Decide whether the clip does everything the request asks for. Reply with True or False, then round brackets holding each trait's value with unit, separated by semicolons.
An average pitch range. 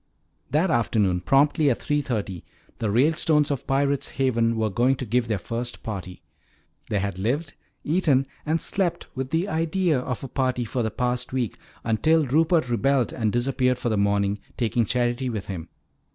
True (4.4 semitones)